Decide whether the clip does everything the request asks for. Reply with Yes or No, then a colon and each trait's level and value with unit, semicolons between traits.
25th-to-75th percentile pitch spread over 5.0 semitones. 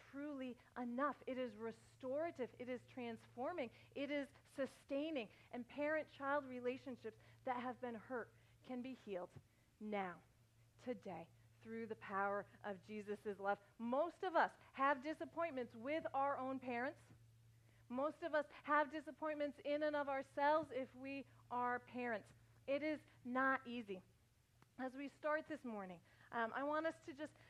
Yes: wide, 5.4 semitones